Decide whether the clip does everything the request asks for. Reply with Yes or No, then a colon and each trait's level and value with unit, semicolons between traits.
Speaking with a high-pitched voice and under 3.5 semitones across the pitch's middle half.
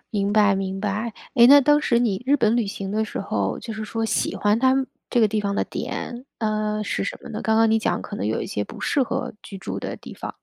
Yes: high, 215 Hz; average, 2.8 semitones